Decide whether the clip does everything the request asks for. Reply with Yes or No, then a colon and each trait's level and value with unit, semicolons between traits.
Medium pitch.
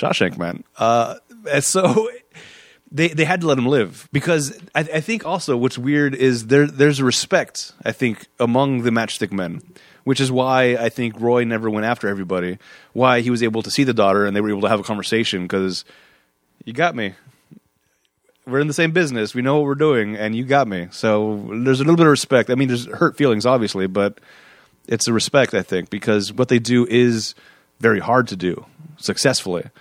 No: low, 120 Hz